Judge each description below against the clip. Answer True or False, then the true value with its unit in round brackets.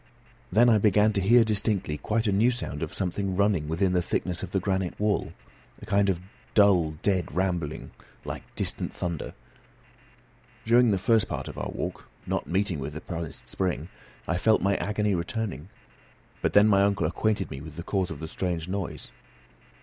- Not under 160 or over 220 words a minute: True (180 wpm)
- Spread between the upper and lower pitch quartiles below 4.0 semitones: True (3.4 semitones)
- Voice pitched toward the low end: True (95 Hz)